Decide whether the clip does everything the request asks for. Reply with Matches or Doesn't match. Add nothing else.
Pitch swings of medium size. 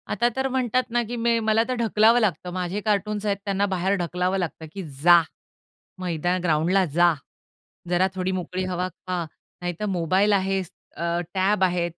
Matches